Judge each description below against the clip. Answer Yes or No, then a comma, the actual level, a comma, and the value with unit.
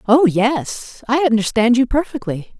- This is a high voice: Yes, high, 245 Hz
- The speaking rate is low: Yes, slow, 115 wpm